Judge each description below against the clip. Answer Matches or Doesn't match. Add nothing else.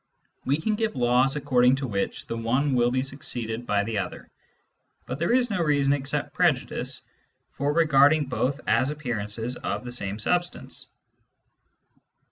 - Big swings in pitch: Doesn't match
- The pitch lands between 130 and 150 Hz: Matches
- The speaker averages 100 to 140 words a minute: Doesn't match